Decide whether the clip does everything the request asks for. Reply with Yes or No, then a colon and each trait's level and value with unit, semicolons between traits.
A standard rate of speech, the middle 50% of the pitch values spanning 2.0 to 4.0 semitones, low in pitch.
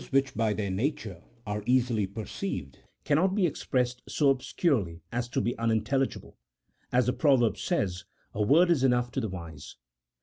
No: average, 175 wpm; average, 4.7 semitones; low, 120 Hz